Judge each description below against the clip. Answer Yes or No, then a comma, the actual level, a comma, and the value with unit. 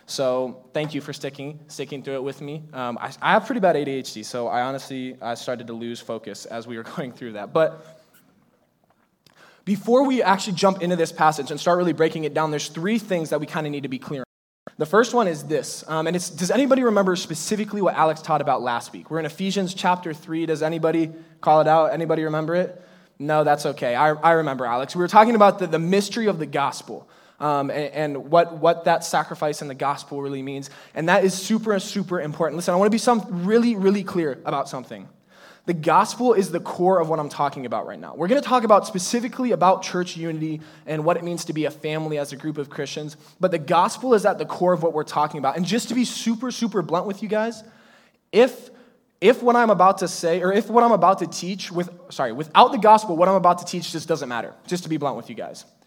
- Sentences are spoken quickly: Yes, fast, 240 wpm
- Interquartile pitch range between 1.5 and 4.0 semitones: No, average, 4.5 semitones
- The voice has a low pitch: No, medium, 165 Hz